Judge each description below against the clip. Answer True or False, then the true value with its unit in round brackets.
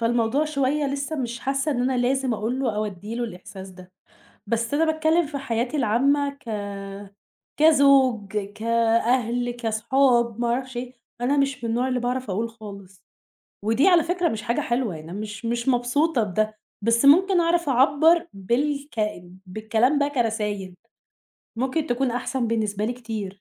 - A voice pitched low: False (245 Hz)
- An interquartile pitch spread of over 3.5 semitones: True (3.9 semitones)